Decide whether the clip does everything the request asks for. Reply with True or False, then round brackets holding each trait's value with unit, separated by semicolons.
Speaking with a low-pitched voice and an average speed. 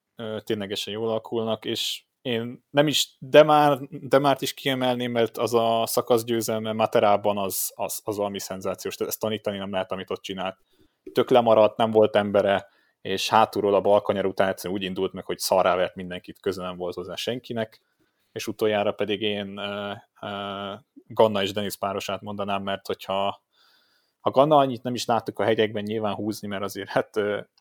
False (105 Hz; 165 wpm)